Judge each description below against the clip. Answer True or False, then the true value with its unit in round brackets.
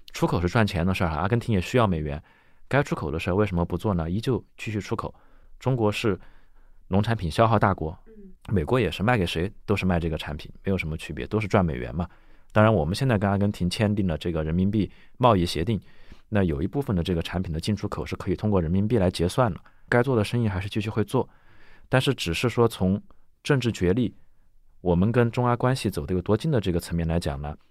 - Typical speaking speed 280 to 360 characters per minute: True (345 characters per minute)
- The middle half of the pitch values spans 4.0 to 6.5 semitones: True (4.6 semitones)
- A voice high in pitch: False (100 Hz)